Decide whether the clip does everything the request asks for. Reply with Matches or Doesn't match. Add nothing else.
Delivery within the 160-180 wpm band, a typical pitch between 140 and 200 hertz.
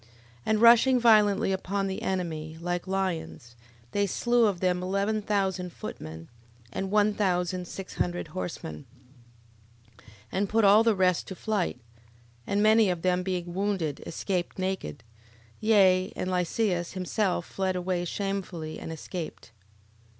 Doesn't match